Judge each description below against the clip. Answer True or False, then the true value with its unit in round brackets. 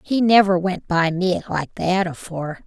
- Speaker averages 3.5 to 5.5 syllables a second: True (4.5 syllables/s)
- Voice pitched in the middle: True (180 Hz)